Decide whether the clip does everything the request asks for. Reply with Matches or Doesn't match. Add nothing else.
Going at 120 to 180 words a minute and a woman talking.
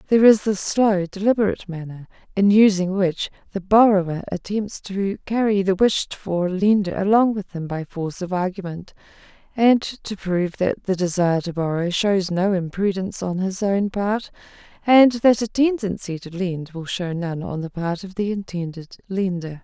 Matches